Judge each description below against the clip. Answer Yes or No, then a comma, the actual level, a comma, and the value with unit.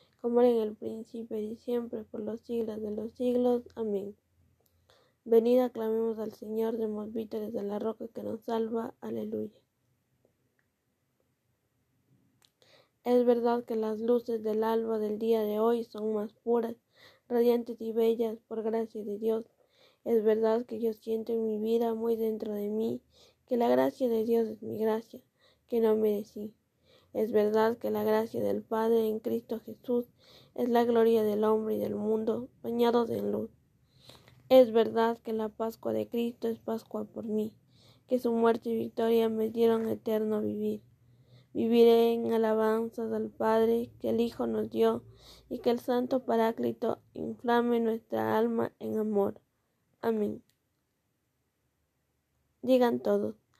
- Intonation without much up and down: Yes, narrow, 1.5 semitones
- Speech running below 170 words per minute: Yes, average, 150 wpm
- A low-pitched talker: No, high, 225 Hz